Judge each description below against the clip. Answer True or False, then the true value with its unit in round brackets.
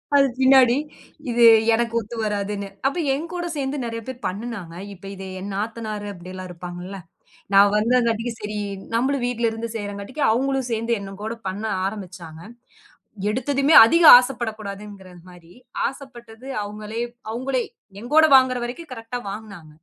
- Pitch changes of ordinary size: True (4.0 semitones)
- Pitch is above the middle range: True (225 Hz)